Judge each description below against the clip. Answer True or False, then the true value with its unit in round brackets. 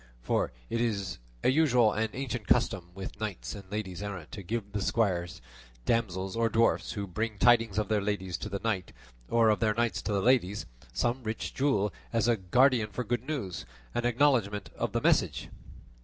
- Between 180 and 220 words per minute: True (185 wpm)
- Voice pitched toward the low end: True (110 Hz)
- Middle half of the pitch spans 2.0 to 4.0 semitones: True (3.2 semitones)